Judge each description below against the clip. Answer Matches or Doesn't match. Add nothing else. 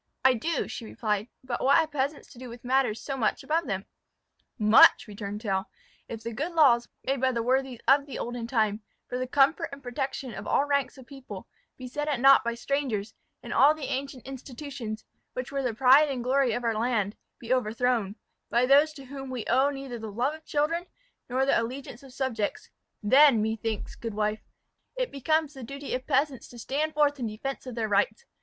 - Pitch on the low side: Doesn't match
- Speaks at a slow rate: Doesn't match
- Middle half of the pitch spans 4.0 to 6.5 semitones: Doesn't match